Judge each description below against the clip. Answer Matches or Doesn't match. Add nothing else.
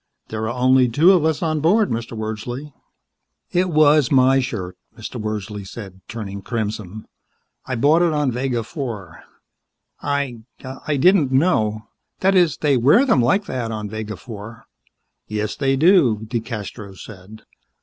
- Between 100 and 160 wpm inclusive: Matches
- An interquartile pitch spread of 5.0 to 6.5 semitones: Matches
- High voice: Doesn't match